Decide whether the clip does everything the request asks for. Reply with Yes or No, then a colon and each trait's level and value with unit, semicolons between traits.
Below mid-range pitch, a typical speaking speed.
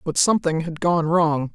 No: medium, 165 Hz; average, 195 wpm